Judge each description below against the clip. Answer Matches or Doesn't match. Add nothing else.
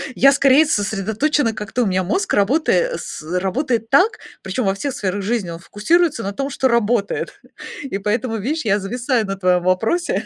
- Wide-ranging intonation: Matches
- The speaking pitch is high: Matches